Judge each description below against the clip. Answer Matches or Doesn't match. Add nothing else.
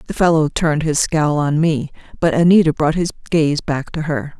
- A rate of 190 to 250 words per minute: Matches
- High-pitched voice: Doesn't match